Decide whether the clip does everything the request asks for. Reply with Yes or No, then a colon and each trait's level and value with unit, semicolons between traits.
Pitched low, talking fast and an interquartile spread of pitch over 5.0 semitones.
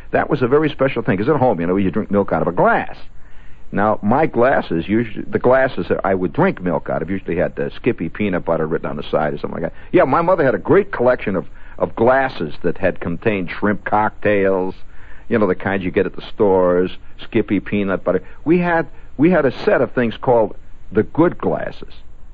Yes: low, 100 Hz; fast, 225 wpm; wide, 5.6 semitones